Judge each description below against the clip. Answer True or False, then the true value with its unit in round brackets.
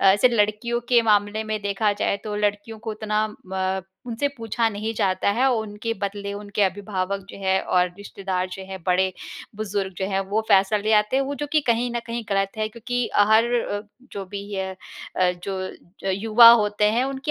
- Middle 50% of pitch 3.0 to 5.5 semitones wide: False (2.4 semitones)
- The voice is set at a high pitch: True (210 Hz)